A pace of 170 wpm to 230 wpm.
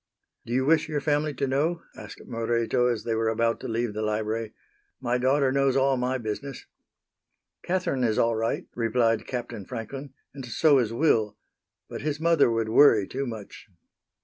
Yes: average, 175 wpm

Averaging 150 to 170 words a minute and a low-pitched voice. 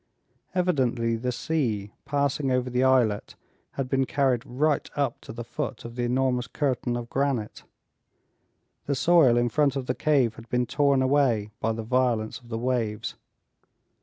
Yes: average, 165 wpm; low, 125 Hz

